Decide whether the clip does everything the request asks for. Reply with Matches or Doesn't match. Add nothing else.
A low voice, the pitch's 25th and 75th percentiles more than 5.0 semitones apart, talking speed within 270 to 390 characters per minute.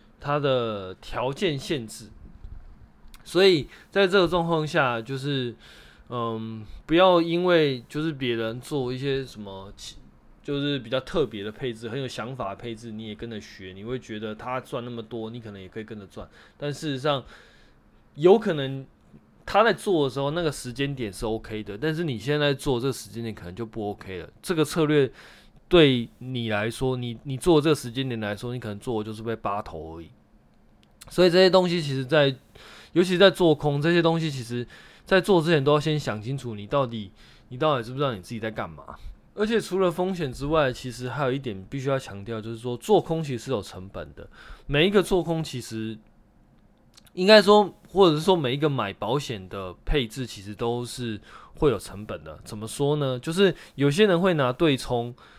Matches